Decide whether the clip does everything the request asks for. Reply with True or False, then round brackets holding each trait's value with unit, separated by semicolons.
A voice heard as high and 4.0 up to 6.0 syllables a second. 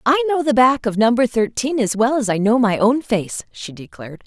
True (225 Hz; 5.0 syllables/s)